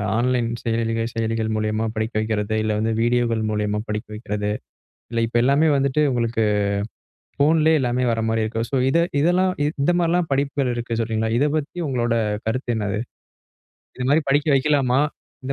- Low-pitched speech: Yes, low, 120 Hz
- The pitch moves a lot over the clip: No, average, 3.8 semitones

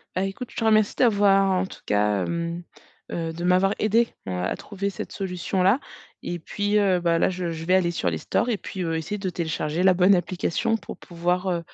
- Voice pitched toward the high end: No, medium, 180 Hz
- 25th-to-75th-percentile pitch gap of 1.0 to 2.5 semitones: No, average, 2.9 semitones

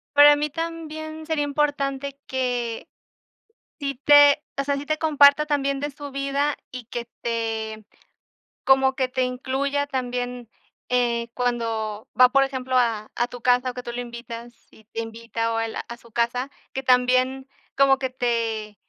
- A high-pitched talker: Yes, very high, 255 Hz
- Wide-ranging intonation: No, average, 3.0 semitones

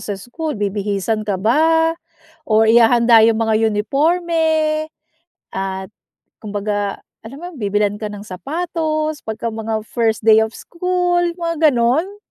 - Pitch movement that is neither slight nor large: No, wide, 6.9 semitones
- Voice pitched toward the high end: Yes, high, 230 Hz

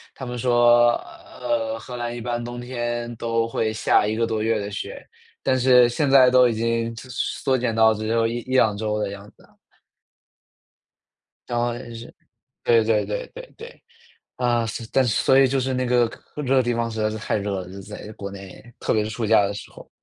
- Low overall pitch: Yes, low, 115 Hz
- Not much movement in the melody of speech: Yes, narrow, 2.1 semitones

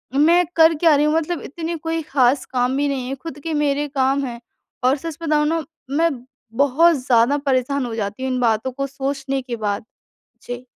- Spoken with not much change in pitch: No, average, 3.3 semitones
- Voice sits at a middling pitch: No, very high, 275 Hz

